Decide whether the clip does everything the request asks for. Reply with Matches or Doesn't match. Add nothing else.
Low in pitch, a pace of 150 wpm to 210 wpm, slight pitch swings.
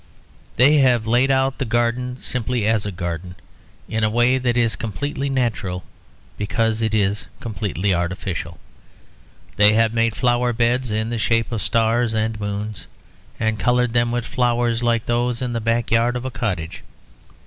Matches